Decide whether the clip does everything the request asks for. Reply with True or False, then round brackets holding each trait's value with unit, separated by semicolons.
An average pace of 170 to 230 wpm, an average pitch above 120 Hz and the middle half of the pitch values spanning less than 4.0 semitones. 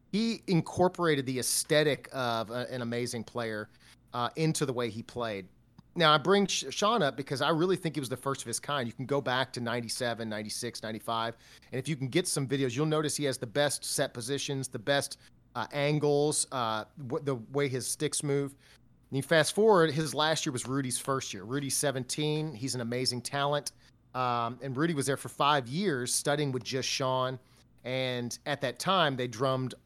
True (200 wpm; 135 Hz; 3.3 semitones)